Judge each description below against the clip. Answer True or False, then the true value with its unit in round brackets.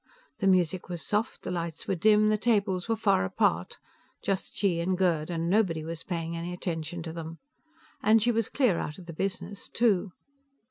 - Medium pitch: True (180 Hz)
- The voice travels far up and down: False (3.7 semitones)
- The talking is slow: False (190 wpm)